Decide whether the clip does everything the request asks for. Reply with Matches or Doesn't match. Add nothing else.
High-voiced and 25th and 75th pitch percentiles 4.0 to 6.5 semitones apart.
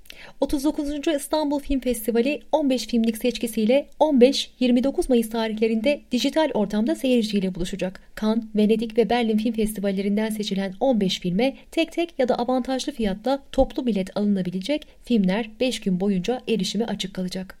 Matches